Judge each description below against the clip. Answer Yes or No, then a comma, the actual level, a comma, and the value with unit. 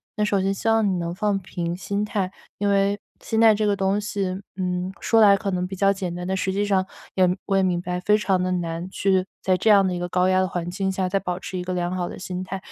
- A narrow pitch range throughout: Yes, narrow, 1.8 semitones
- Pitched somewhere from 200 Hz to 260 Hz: No, high, 190 Hz